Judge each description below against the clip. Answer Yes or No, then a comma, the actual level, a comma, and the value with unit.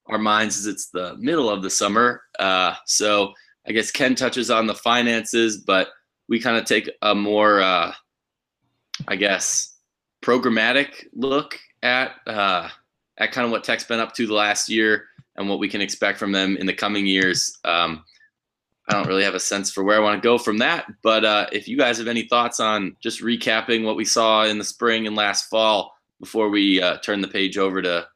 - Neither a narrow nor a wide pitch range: No, narrow, 2.3 semitones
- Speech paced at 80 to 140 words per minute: No, fast, 205 wpm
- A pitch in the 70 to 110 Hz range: Yes, low, 105 Hz